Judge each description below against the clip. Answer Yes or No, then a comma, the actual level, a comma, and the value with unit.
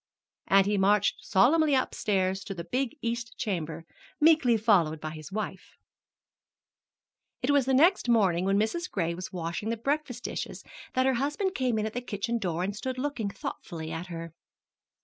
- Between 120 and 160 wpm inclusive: No, average, 170 wpm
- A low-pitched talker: No, high, 215 Hz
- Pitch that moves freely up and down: Yes, wide, 5.9 semitones